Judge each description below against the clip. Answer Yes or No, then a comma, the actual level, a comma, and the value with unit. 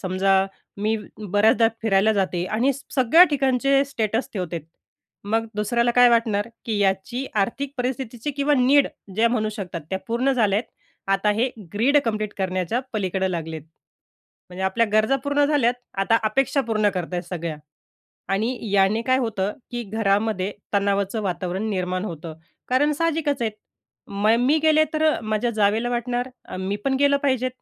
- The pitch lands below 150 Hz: No, high, 220 Hz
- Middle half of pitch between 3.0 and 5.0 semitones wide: Yes, average, 4.5 semitones